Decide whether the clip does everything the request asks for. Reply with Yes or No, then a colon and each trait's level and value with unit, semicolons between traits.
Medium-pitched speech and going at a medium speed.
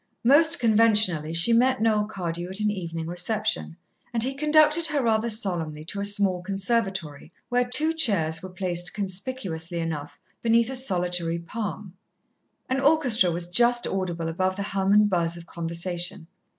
No: high, 195 Hz; average, 155 wpm